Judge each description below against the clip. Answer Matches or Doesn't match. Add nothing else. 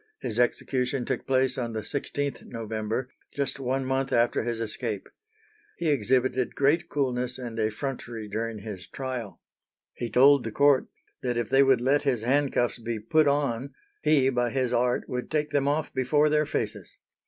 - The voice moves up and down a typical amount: Matches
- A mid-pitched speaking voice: Doesn't match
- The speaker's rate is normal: Matches